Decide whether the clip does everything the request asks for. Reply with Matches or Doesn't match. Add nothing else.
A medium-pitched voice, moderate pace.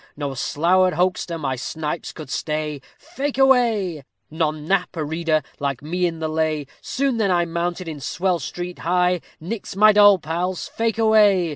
Matches